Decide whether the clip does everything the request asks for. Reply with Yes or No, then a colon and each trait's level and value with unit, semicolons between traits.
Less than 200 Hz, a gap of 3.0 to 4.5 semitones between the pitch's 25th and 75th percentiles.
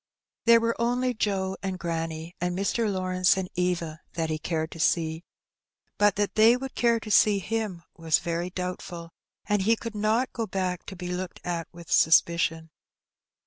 Yes: medium, 185 Hz; average, 4.0 semitones